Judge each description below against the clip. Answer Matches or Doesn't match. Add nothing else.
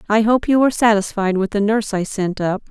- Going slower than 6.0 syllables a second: Doesn't match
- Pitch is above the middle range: Matches